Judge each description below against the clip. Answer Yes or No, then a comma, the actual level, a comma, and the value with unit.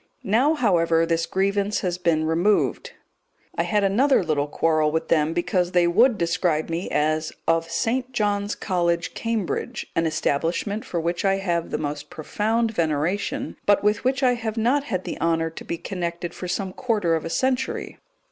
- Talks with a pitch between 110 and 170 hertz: No, medium, 180 Hz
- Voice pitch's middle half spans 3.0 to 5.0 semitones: Yes, average, 4.3 semitones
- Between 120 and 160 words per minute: No, average, 175 wpm